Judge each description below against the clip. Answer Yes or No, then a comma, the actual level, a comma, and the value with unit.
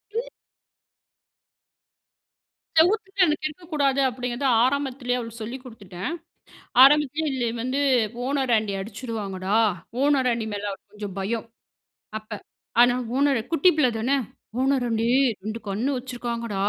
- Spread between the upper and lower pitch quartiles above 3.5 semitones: Yes, average, 4.2 semitones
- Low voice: No, high, 245 Hz